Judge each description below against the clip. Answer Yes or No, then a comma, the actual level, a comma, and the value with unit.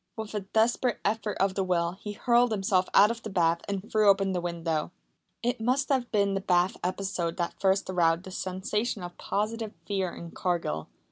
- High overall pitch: Yes, high, 195 Hz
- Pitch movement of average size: Yes, average, 3.4 semitones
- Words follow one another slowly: No, average, 195 wpm